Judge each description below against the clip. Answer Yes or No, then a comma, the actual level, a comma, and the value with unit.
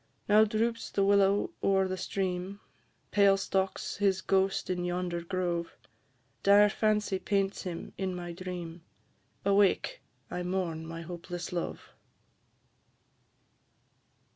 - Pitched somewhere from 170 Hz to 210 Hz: Yes, high, 190 Hz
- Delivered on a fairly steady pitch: Yes, narrow, 2.1 semitones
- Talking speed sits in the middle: No, slow, 115 wpm